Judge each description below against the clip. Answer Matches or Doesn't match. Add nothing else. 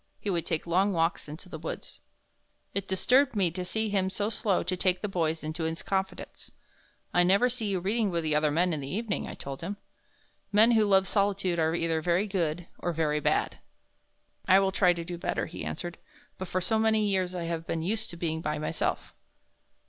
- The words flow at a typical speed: Doesn't match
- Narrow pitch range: Doesn't match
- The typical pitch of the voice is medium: Matches